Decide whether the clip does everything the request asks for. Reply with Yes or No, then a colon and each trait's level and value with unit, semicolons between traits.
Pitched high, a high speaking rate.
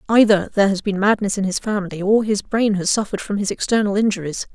Yes: high, 205 Hz; fast, 225 wpm